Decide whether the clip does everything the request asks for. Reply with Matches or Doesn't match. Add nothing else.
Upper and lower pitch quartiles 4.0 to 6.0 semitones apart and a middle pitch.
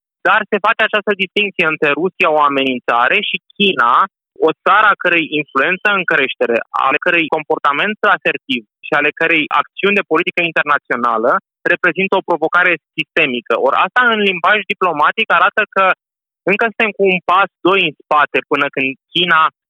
Matches